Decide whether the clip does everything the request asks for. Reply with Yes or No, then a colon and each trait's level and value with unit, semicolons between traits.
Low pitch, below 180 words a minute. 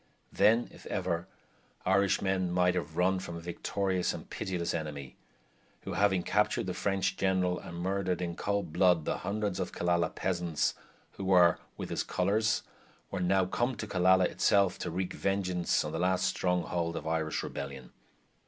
Yes: very low, 90 Hz; average, 160 wpm